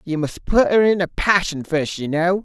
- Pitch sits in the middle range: Yes, medium, 175 Hz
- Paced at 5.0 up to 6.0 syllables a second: No, 4.7 syllables/s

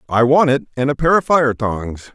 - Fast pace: Yes, fast, 250 wpm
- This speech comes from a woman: No, male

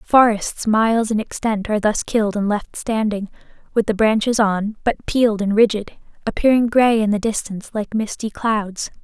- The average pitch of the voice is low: No, high, 215 Hz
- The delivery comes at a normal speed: Yes, average, 175 wpm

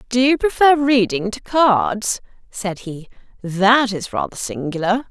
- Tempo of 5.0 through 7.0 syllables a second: No, 4.0 syllables/s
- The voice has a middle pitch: No, high, 225 Hz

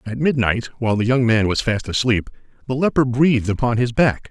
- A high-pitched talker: No, low, 120 Hz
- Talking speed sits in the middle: No, fast, 210 wpm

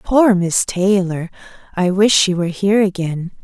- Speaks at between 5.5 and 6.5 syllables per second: No, 4.7 syllables/s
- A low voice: No, high, 190 Hz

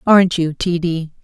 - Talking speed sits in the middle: Yes, average, 195 wpm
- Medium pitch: Yes, medium, 170 Hz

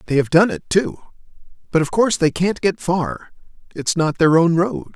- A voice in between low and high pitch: Yes, medium, 165 Hz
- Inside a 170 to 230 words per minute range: Yes, fast, 205 wpm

